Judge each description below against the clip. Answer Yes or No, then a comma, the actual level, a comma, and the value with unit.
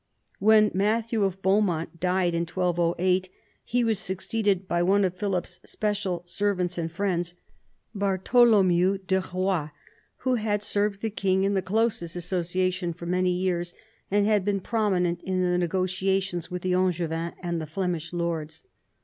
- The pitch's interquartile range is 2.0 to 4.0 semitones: Yes, narrow, 2.4 semitones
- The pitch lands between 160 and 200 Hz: Yes, medium, 185 Hz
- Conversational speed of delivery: Yes, average, 150 wpm